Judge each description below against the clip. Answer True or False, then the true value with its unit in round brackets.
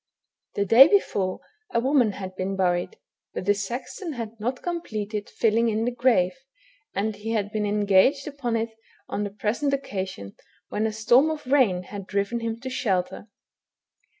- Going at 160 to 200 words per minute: True (165 wpm)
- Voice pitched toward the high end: True (220 Hz)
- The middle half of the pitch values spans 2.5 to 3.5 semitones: False (4.0 semitones)